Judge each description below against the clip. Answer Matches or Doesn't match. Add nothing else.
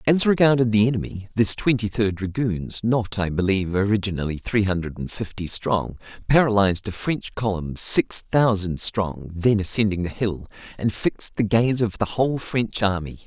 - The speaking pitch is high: Doesn't match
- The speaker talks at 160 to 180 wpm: Matches